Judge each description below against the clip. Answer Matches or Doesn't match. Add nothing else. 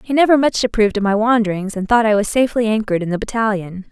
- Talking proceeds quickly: Matches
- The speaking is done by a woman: Matches